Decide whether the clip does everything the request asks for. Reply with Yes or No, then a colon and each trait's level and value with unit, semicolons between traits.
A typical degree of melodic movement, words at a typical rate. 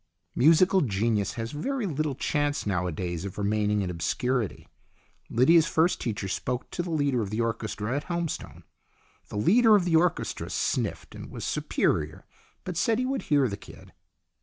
No: wide, 8.1 semitones; average, 160 wpm